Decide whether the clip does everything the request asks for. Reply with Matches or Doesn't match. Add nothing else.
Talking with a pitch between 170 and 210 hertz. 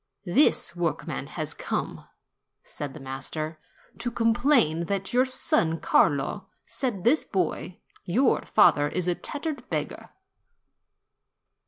Matches